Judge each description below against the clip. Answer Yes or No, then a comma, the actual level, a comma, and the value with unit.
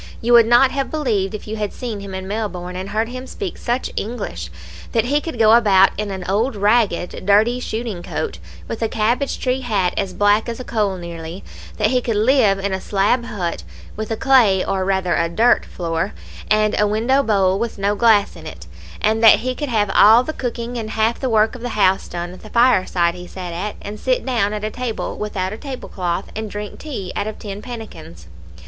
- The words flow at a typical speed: No, fast, 220 wpm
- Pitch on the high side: Yes, high, 215 Hz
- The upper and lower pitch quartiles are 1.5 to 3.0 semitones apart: No, average, 3.7 semitones